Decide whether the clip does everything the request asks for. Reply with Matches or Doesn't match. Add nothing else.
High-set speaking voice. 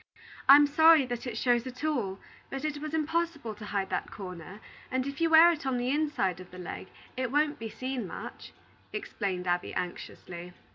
Matches